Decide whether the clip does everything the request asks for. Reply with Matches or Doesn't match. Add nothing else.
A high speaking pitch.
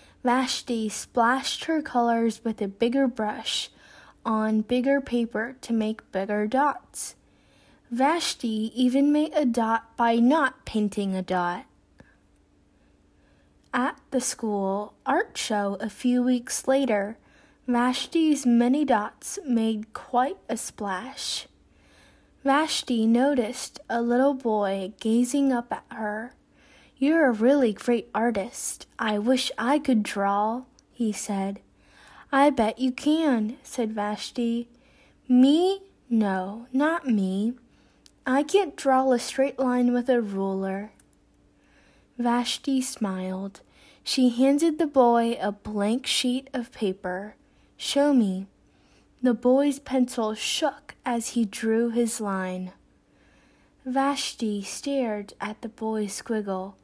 Matches